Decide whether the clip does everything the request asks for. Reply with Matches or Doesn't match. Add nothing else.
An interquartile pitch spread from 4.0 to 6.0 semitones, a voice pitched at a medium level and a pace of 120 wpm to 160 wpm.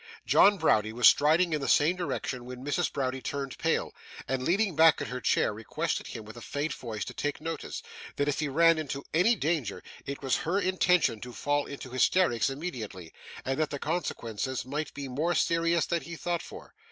Doesn't match